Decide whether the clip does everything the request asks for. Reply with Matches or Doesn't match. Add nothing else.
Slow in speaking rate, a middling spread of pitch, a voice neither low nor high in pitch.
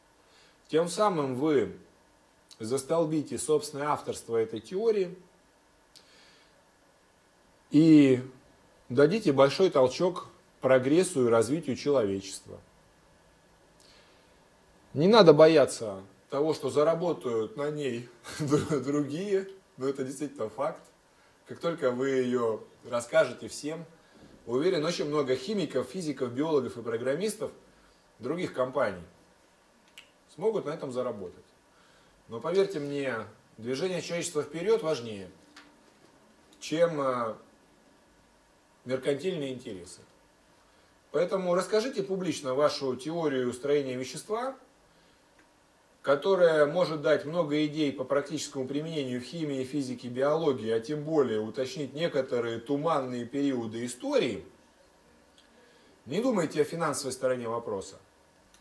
Matches